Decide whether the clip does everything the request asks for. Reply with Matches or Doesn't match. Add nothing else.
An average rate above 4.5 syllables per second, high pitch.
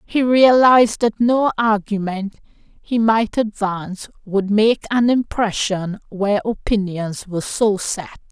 Doesn't match